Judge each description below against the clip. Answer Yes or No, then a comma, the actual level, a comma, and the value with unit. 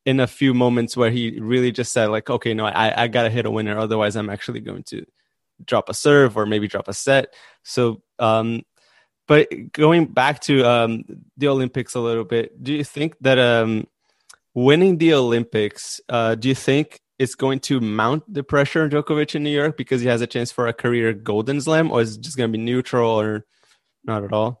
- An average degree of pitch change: Yes, average, 3.6 semitones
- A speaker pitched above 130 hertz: No, low, 120 Hz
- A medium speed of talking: No, fast, 210 wpm